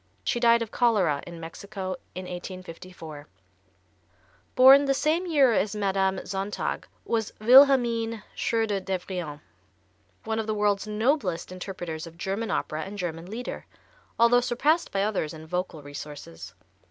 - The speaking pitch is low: No, high, 200 Hz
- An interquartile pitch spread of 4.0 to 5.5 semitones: Yes, average, 4.7 semitones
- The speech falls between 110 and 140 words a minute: Yes, slow, 135 wpm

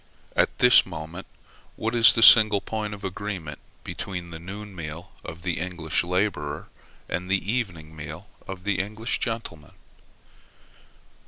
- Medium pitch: No, very low, 95 Hz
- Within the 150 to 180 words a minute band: No, average, 140 wpm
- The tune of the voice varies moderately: Yes, average, 4.1 semitones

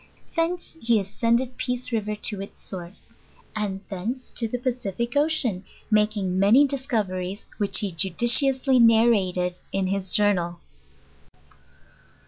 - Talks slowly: Yes, slow, 120 wpm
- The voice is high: Yes, high, 215 Hz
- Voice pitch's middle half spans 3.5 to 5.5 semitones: Yes, average, 4.4 semitones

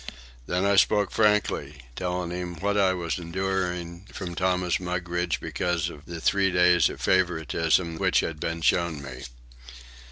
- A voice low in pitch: Yes, very low, 90 Hz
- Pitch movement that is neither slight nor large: No, narrow, 1.9 semitones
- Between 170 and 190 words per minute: No, average, 150 wpm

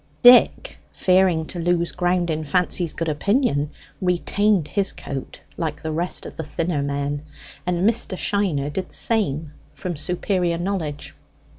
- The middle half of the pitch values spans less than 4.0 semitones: Yes, average, 3.5 semitones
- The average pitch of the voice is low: No, medium, 175 Hz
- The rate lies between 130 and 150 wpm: Yes, average, 145 wpm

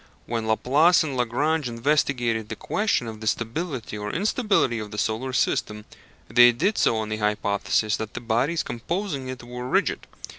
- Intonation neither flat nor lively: Yes, average, 4.7 semitones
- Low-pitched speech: Yes, low, 120 Hz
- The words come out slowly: No, average, 170 wpm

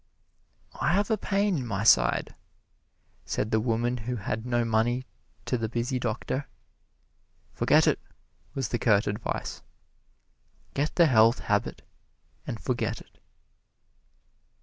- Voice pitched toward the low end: Yes, low, 120 Hz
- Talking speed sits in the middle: No, slow, 125 wpm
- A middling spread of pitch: Yes, average, 3.0 semitones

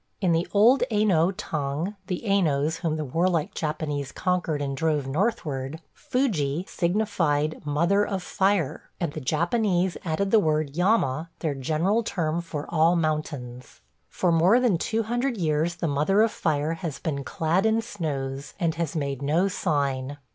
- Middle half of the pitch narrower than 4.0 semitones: No, average, 4.7 semitones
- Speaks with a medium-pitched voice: Yes, medium, 165 Hz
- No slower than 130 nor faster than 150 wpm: No, average, 160 wpm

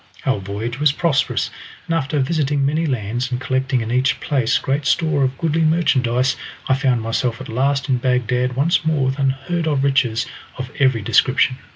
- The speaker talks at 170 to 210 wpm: Yes, average, 180 wpm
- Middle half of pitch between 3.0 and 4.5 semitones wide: No, narrow, 2.5 semitones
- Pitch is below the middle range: Yes, low, 130 Hz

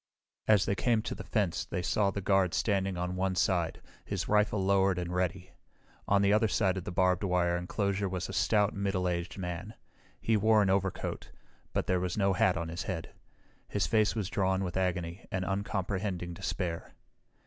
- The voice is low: Yes, very low, 95 Hz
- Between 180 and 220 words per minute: Yes, average, 190 wpm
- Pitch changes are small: Yes, narrow, 1.9 semitones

